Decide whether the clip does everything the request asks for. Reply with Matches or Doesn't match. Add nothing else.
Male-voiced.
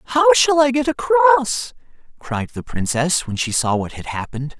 Matches